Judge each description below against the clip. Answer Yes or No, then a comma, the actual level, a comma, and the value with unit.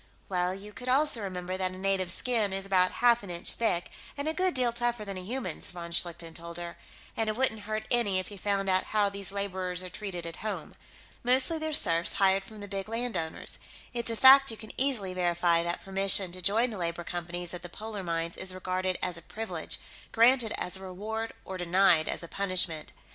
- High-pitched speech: Yes, high, 195 Hz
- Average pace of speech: No, fast, 215 wpm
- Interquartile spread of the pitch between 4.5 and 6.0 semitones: No, average, 3.8 semitones